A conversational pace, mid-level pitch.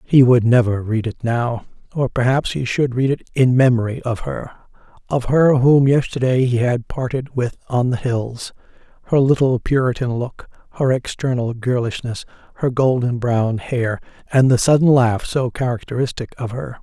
No: average, 160 wpm; low, 125 Hz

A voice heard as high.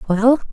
Yes: high, 230 Hz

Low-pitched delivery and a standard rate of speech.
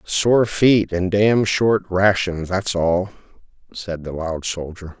Yes: very low, 95 Hz; average, 145 wpm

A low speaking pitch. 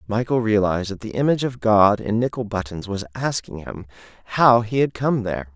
Yes: low, 110 Hz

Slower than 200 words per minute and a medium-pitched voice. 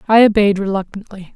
No: slow, 135 wpm; high, 200 Hz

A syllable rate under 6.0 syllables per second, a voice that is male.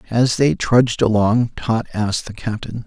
Yes: 4.7 syllables/s; male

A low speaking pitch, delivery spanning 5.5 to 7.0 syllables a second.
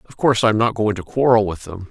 Yes: low, 110 Hz; 6.9 syllables/s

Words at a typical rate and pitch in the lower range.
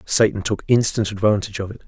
Yes: average, 190 wpm; low, 105 Hz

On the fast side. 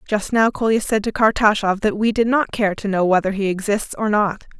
Yes: fast, 235 wpm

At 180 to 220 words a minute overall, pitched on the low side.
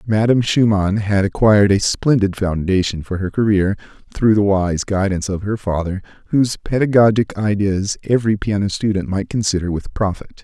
No: average, 155 wpm; low, 100 Hz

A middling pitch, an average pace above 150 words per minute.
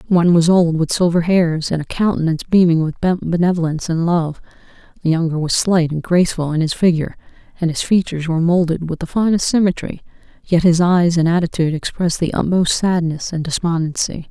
Yes: medium, 170 Hz; average, 180 wpm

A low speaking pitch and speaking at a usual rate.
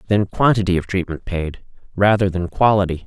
Yes: very low, 95 Hz; average, 155 wpm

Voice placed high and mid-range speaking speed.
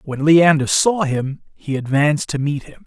No: medium, 150 Hz; average, 190 wpm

